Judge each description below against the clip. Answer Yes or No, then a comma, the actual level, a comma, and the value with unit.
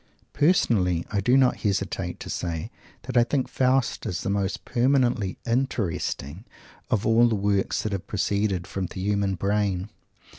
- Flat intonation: No, average, 3.9 semitones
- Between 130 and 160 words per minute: Yes, average, 155 wpm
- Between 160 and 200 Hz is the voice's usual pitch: No, low, 100 Hz